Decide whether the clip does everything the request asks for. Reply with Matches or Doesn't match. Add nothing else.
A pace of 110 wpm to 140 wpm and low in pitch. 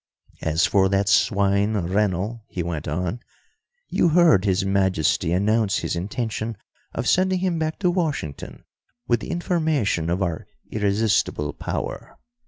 Matches